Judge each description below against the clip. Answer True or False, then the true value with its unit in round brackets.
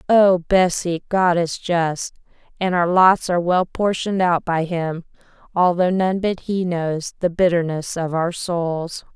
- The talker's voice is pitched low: False (175 Hz)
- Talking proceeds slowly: False (155 wpm)